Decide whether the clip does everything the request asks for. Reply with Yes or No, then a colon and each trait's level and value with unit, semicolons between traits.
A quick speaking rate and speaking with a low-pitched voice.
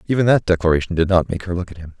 Yes: fast, 300 wpm; very low, 90 Hz